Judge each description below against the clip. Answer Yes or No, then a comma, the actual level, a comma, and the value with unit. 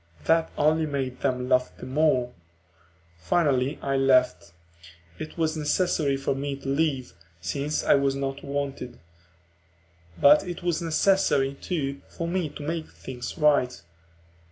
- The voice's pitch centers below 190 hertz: Yes, medium, 140 Hz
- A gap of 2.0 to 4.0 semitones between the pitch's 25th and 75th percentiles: Yes, average, 2.8 semitones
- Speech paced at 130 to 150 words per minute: Yes, slow, 135 wpm